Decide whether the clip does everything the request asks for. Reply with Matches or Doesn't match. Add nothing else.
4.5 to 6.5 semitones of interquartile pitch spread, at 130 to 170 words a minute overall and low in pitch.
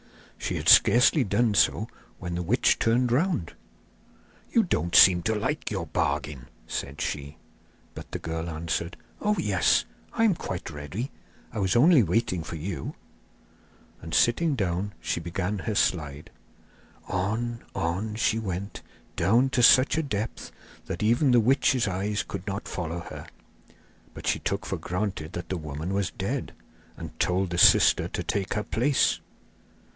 Matches